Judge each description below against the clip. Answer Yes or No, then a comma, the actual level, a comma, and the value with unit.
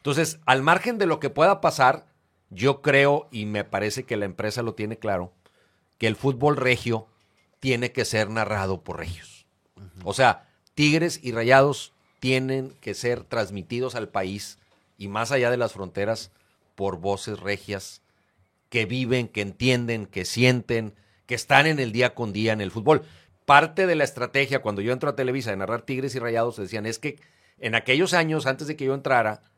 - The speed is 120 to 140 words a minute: No, average, 185 wpm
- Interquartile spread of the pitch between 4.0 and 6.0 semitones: Yes, average, 4.6 semitones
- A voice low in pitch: Yes, low, 115 Hz